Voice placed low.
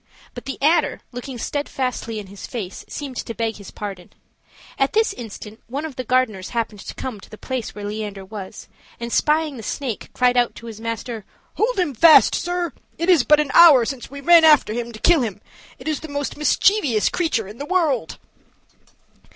No: very high, 250 Hz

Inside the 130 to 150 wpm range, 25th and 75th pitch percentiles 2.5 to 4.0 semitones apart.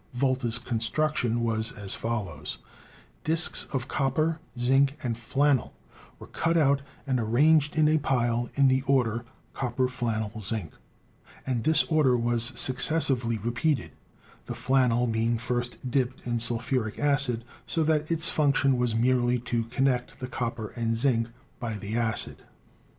Yes: average, 140 wpm; average, 2.9 semitones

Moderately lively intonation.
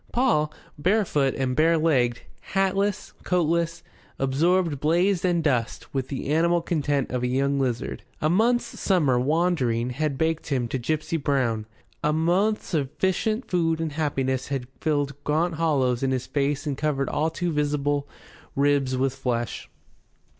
Yes: average, 3.9 semitones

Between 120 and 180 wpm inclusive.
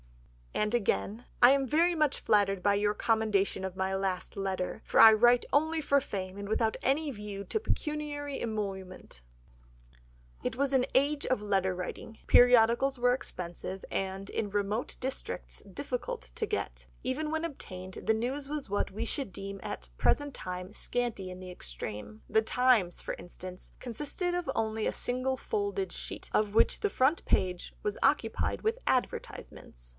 Yes: average, 165 wpm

